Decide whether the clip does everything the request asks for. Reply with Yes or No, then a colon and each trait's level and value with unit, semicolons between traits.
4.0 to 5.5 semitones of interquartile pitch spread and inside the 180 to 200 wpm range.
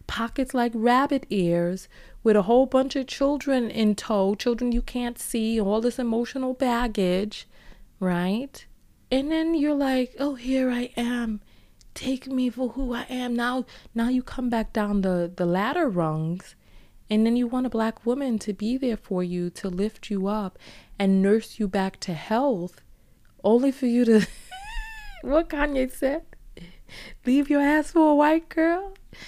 No: average, 4.3 semitones; average, 165 wpm